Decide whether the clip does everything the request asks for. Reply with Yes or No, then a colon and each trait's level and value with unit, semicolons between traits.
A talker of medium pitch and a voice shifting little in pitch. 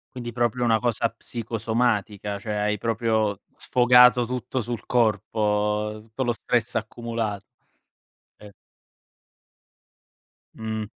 No: low, 115 Hz; narrow, 2.2 semitones